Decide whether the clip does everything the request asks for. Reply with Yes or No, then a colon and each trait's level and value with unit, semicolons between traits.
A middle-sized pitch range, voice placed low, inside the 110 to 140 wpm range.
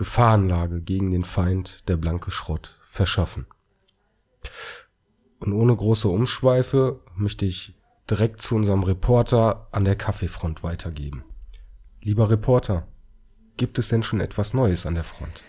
Yes: average, 4.1 semitones; low, 100 Hz; average, 130 wpm